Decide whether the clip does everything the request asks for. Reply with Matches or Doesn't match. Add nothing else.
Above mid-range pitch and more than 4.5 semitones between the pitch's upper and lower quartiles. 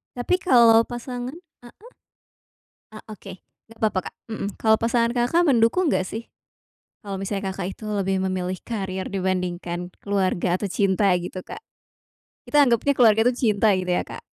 Doesn't match